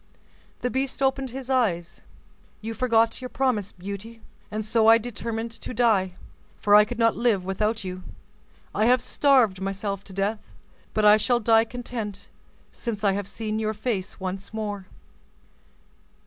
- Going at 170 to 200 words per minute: No, average, 155 wpm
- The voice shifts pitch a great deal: No, average, 3.0 semitones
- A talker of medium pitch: No, high, 220 Hz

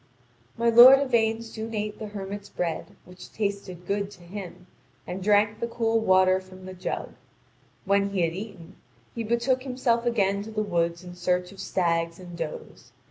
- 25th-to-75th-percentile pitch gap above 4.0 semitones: No, average, 3.7 semitones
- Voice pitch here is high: Yes, high, 200 Hz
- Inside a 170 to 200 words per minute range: Yes, average, 175 wpm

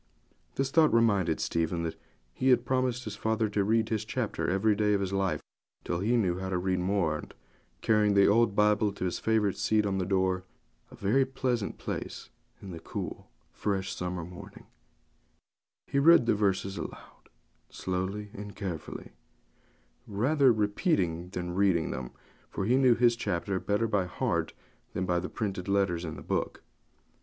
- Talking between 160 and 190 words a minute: Yes, average, 170 wpm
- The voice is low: Yes, low, 100 Hz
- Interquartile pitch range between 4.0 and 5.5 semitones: No, average, 3.3 semitones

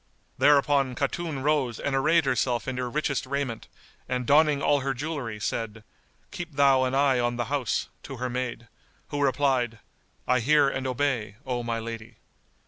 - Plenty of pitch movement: No, average, 2.9 semitones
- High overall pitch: No, low, 130 Hz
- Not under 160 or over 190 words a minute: Yes, average, 165 wpm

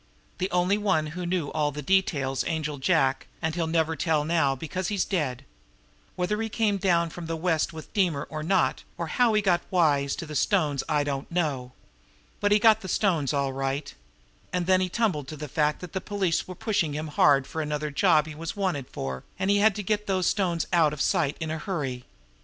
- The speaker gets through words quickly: Yes, fast, 215 wpm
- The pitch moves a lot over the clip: No, average, 4.2 semitones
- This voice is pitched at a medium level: Yes, medium, 165 Hz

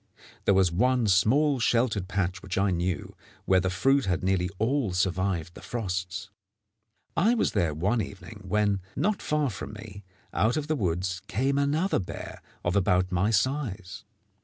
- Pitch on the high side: No, low, 100 Hz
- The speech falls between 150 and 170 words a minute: Yes, average, 160 wpm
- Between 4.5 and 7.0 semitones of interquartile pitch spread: Yes, average, 5.2 semitones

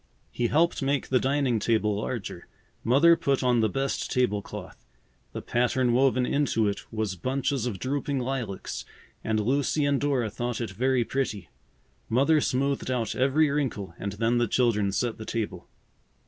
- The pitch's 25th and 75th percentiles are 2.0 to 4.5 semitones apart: Yes, average, 3.8 semitones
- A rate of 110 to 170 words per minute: Yes, average, 160 wpm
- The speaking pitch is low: Yes, low, 125 Hz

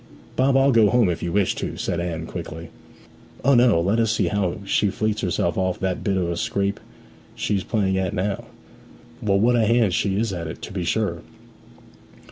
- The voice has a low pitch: Yes, low, 100 Hz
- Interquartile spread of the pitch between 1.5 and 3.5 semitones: No, average, 3.9 semitones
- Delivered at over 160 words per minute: Yes, average, 200 wpm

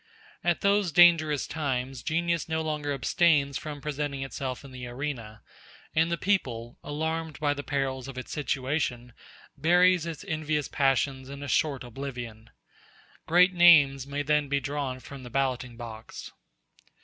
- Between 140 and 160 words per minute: Yes, average, 150 wpm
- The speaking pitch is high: No, medium, 140 Hz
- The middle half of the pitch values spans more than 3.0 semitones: Yes, average, 3.4 semitones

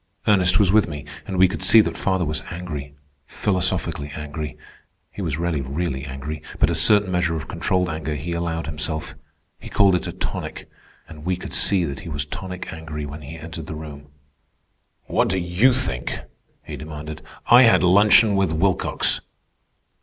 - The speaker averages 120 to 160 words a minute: No, average, 175 wpm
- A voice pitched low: Yes, very low, 80 Hz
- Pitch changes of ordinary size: Yes, average, 3.6 semitones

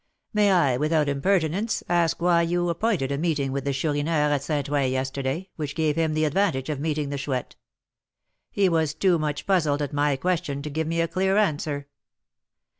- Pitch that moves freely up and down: No, average, 3.2 semitones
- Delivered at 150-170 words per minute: No, average, 190 wpm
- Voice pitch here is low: No, medium, 155 Hz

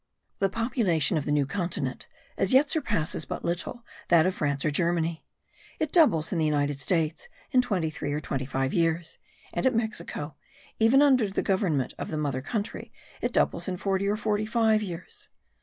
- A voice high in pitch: No, medium, 175 Hz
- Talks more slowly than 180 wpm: No, average, 185 wpm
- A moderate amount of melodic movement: No, wide, 6.0 semitones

